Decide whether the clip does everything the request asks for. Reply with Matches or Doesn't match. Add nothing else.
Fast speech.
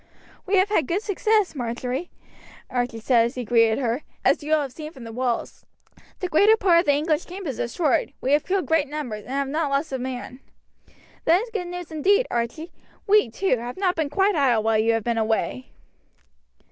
Matches